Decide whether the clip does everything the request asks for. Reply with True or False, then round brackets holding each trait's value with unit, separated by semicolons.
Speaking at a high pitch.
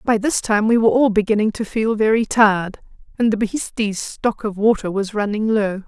True (215 Hz)